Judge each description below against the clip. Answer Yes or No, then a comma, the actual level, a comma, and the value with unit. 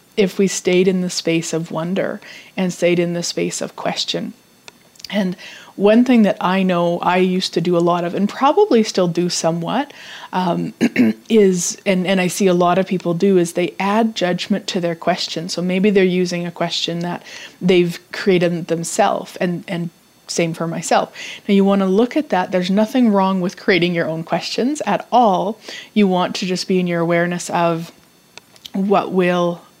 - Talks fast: No, average, 190 wpm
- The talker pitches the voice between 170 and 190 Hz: Yes, medium, 185 Hz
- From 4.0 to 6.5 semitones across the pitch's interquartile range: No, narrow, 2.5 semitones